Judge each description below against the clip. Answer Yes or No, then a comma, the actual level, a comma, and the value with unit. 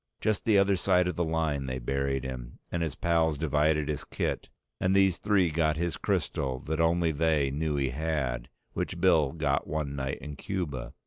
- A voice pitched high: No, very low, 80 Hz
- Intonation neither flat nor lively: Yes, average, 3.6 semitones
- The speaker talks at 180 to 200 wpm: Yes, average, 190 wpm